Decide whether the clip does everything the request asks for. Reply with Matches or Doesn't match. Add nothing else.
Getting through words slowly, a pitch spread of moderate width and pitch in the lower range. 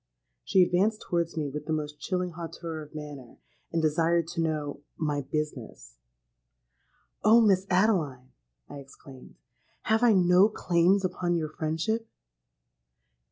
Doesn't match